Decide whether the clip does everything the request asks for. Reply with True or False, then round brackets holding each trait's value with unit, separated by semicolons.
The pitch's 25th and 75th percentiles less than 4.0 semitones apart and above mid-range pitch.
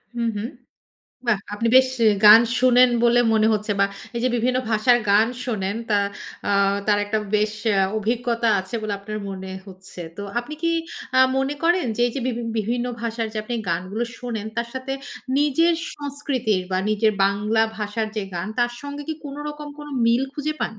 True (3.5 semitones; 230 Hz)